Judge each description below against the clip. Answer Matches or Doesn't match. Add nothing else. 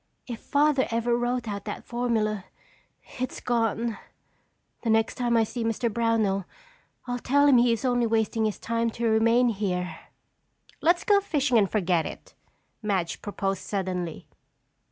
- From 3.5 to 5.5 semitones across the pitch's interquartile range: Doesn't match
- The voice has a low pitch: Doesn't match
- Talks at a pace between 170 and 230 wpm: Doesn't match